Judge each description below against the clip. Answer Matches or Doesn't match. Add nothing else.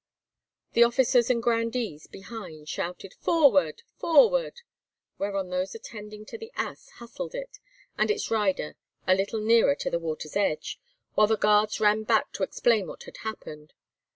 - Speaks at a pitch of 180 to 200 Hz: Doesn't match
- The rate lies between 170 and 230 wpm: Doesn't match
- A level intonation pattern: Doesn't match